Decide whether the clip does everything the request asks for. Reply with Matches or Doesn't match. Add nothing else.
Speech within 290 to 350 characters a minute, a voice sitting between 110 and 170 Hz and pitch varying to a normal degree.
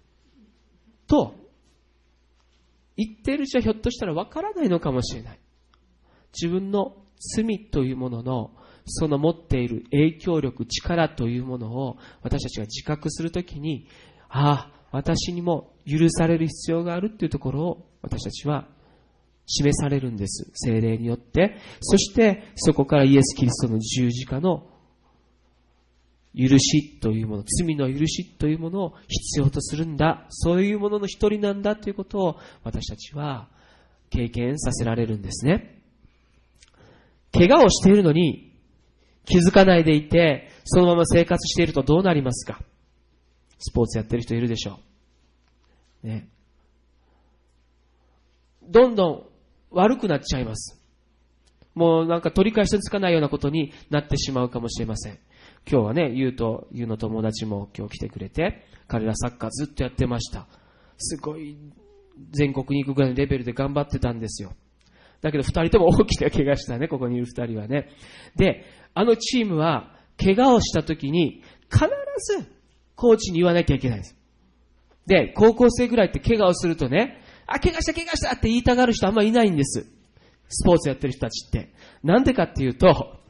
Doesn't match